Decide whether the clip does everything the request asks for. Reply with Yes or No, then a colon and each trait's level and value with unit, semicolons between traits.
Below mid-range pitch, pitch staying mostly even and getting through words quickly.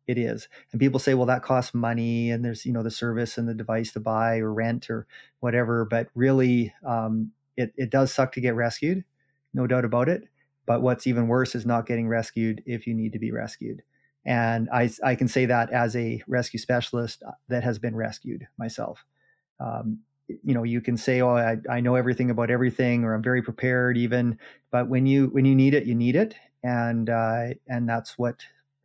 Yes: low, 120 Hz; narrow, 1.6 semitones; fast, 210 wpm